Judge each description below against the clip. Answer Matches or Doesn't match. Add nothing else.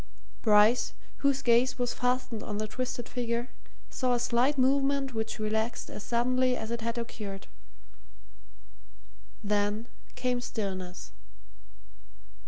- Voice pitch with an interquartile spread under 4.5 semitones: Matches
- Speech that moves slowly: Matches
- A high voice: Matches